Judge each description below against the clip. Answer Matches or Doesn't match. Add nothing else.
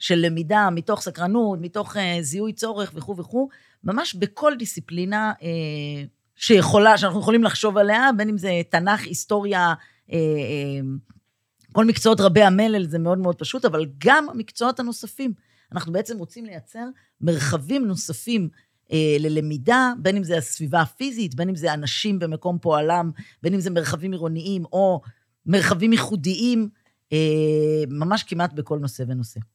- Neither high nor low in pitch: Matches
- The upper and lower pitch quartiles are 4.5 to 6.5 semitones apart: Matches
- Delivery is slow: Doesn't match